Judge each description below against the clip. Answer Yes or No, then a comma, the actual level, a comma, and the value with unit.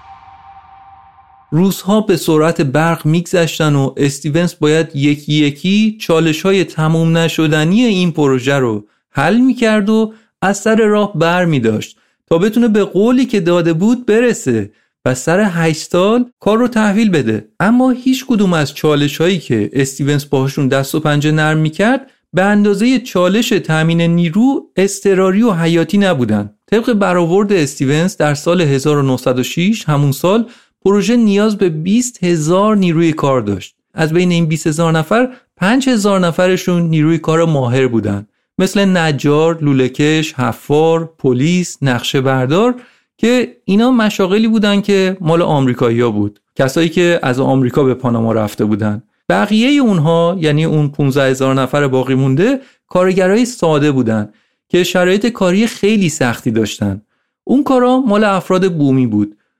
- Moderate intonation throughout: No, wide, 6.6 semitones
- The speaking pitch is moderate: Yes, medium, 165 Hz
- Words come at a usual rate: Yes, average, 140 wpm